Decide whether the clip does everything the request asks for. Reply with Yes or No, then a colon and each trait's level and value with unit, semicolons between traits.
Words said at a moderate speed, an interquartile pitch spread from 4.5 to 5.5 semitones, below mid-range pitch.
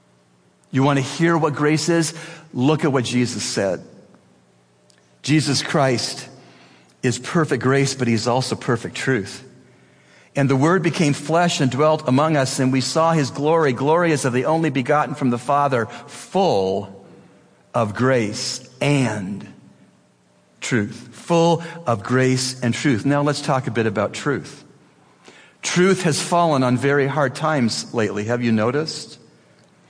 Yes: average, 145 wpm; average, 4.9 semitones; low, 130 Hz